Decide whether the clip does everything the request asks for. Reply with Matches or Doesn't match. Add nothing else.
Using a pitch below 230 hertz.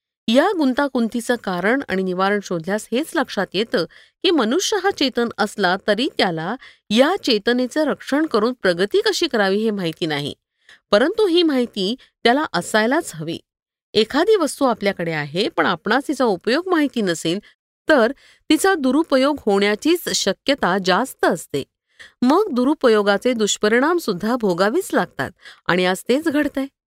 Doesn't match